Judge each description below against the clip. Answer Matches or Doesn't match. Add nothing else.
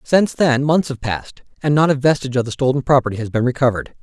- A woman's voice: Doesn't match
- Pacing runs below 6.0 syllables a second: Doesn't match